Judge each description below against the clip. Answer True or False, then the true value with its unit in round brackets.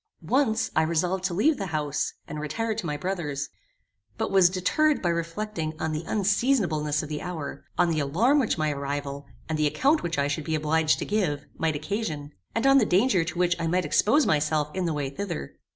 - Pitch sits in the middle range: True (165 Hz)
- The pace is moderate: False (210 wpm)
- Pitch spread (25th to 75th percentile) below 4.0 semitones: False (5.0 semitones)